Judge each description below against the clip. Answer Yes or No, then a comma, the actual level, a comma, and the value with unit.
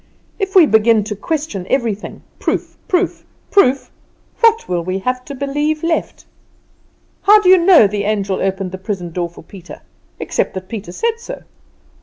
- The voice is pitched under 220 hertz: No, high, 225 Hz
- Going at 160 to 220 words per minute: Yes, average, 165 wpm